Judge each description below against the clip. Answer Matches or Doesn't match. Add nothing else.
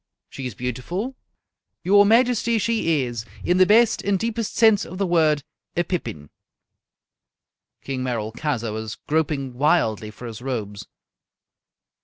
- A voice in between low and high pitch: Matches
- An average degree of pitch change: Doesn't match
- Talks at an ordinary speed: Doesn't match